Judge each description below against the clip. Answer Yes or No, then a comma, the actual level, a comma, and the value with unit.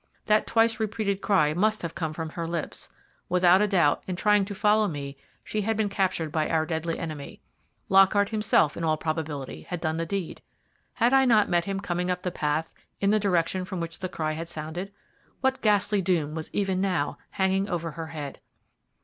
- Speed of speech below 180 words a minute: No, average, 195 wpm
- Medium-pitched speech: Yes, medium, 180 Hz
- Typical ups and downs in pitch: Yes, average, 3.9 semitones